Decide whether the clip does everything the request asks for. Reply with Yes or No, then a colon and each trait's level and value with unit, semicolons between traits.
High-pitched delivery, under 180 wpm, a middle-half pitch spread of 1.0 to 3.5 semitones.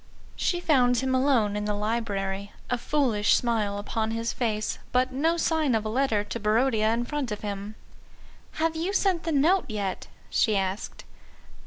No: high, 230 Hz; average, 170 wpm; average, 4.8 semitones